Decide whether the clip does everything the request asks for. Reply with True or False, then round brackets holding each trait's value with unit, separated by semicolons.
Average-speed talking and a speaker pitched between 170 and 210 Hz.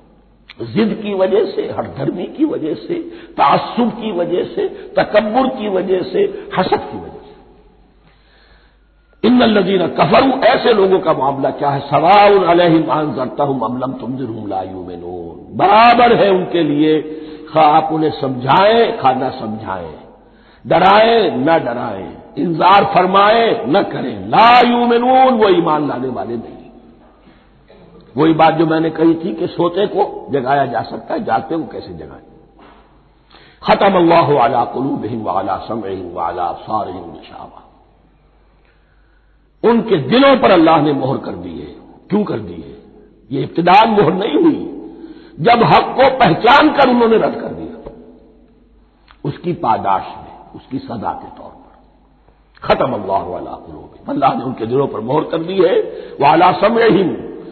True (145 wpm; 190 Hz)